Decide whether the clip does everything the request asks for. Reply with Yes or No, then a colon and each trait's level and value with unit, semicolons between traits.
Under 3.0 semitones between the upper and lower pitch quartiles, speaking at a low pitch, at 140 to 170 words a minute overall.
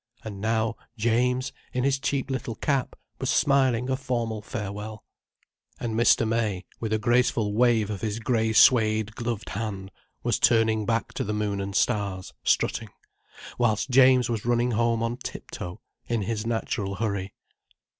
Yes: narrow, 2.4 semitones; low, 115 Hz; average, 155 wpm